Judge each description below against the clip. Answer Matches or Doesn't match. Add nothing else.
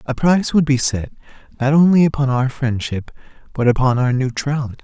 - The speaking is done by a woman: Doesn't match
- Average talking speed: Matches